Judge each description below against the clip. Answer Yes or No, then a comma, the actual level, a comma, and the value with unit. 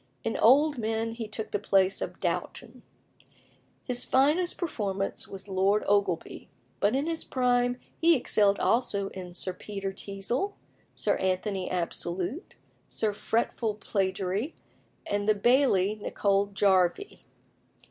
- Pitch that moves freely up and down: No, average, 4.1 semitones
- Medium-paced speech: No, slow, 125 wpm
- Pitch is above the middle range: Yes, high, 205 Hz